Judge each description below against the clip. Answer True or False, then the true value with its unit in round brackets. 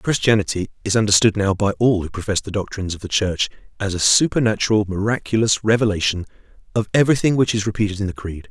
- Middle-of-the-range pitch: False (105 Hz)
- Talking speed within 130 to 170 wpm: False (185 wpm)